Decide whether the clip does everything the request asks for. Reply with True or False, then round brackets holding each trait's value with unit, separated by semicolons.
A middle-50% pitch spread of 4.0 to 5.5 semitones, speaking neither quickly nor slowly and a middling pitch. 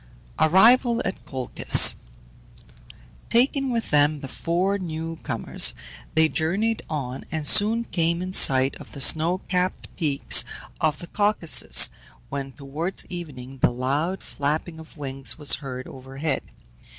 False (5.1 semitones; 130 wpm; 160 Hz)